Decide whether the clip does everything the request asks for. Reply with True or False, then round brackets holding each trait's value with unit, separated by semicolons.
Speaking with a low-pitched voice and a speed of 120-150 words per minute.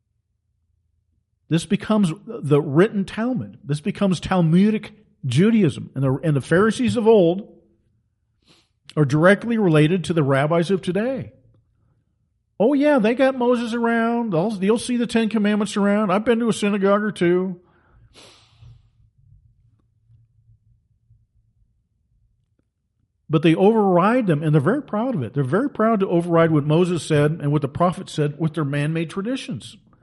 False (165 Hz; 140 wpm)